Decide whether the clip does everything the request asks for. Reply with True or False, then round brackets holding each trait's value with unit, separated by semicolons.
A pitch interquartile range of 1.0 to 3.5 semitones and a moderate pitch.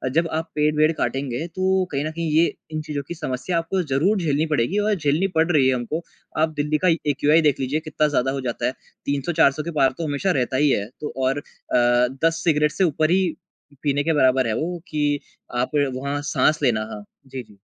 True (3.2 semitones; 150 Hz)